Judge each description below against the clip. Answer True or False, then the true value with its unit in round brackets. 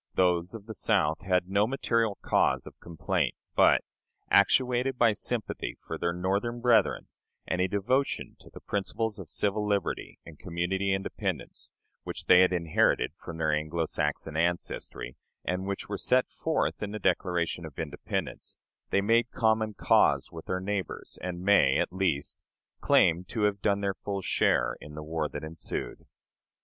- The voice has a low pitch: True (95 Hz)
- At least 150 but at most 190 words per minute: True (160 wpm)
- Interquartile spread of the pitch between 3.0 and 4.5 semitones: True (3.7 semitones)